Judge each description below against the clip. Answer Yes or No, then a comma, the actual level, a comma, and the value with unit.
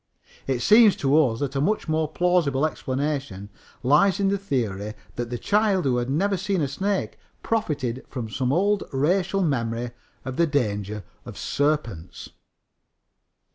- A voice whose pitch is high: No, medium, 145 Hz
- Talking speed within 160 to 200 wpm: No, average, 150 wpm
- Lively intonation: Yes, wide, 7.3 semitones